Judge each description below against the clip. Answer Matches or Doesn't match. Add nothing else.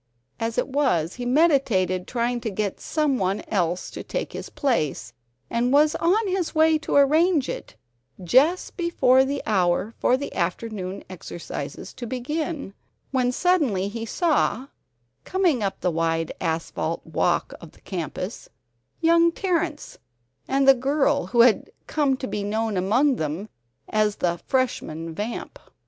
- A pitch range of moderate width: Doesn't match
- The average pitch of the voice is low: Doesn't match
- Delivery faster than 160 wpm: Doesn't match